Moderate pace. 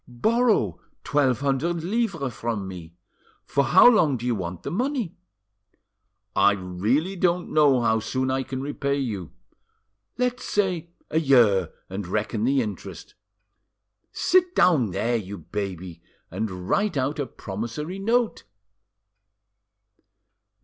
No: slow, 125 wpm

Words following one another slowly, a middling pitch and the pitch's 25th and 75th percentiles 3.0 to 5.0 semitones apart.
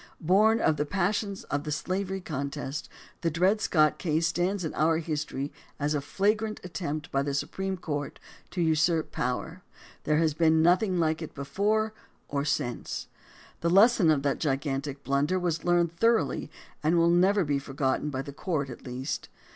No: average, 180 wpm; medium, 160 Hz; average, 4.3 semitones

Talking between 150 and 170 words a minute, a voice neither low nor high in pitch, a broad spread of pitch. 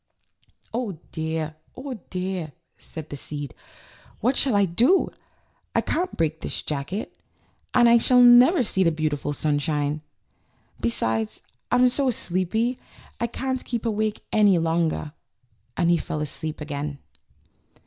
No: slow, 135 wpm; medium, 175 Hz; wide, 7.7 semitones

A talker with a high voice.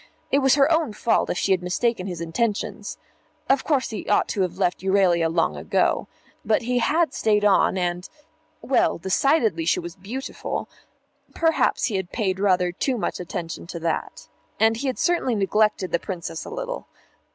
Yes: high, 200 Hz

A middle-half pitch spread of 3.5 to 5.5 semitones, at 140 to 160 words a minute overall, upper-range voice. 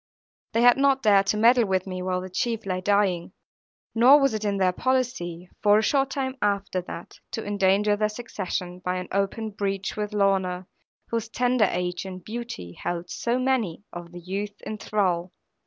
No: average, 3.9 semitones; average, 185 wpm; high, 200 Hz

